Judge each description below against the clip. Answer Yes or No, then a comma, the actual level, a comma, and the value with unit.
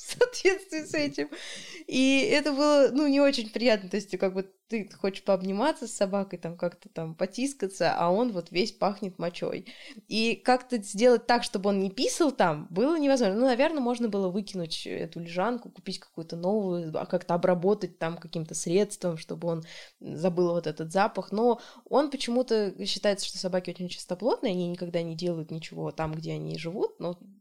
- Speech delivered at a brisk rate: Yes, fast, 175 wpm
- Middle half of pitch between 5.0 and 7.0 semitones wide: Yes, wide, 5.6 semitones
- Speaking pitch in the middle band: No, high, 195 Hz